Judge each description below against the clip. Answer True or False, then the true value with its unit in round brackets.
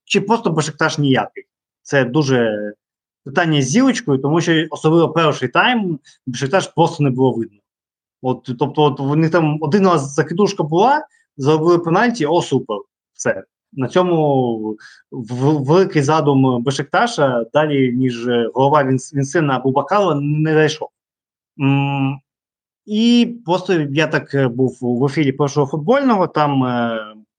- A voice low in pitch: False (150 Hz)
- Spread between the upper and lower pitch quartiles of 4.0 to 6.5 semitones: True (4.5 semitones)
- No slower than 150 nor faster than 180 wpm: False (130 wpm)